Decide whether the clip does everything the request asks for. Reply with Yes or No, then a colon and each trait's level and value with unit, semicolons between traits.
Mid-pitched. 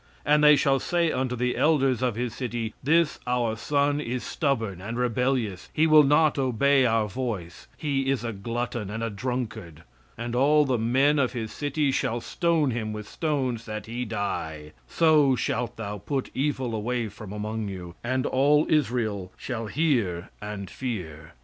No: low, 125 Hz